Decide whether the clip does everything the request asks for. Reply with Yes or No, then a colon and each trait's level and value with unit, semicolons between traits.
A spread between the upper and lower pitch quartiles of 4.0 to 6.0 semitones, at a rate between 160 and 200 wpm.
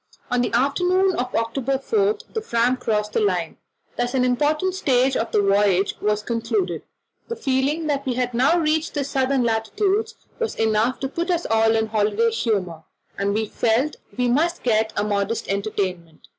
Yes: average, 4.9 semitones; average, 175 wpm